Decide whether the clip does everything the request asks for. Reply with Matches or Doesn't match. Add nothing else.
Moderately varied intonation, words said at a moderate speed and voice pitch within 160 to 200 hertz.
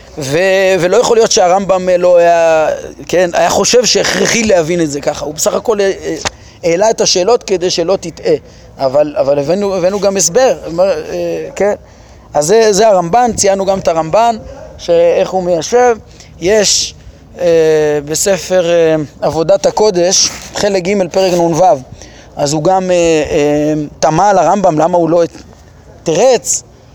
Matches